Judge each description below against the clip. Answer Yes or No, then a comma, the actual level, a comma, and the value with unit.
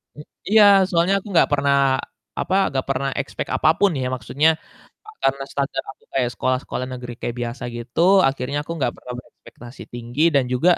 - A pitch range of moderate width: Yes, average, 3.0 semitones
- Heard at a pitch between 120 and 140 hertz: Yes, low, 135 Hz